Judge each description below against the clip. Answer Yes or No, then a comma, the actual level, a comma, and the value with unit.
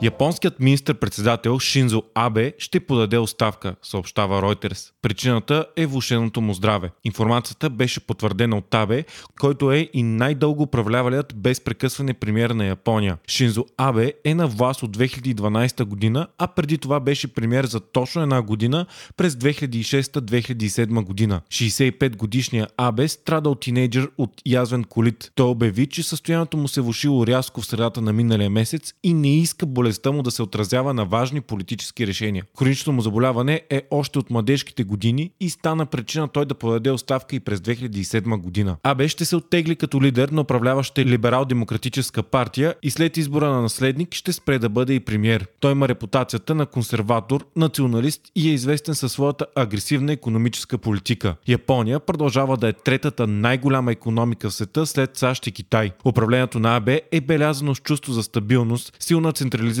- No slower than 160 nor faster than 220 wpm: Yes, fast, 165 wpm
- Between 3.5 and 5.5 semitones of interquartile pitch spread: Yes, average, 4.0 semitones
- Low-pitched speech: Yes, low, 125 Hz